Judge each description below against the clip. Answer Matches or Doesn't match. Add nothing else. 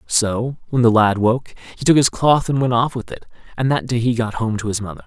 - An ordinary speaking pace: Doesn't match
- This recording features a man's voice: Matches